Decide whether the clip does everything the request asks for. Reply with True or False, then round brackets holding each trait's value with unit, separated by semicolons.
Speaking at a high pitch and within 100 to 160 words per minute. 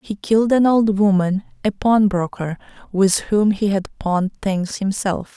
True (200 Hz; 155 wpm)